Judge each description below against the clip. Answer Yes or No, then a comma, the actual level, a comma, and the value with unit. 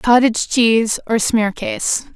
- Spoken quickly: No, slow, 110 wpm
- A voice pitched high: Yes, high, 225 Hz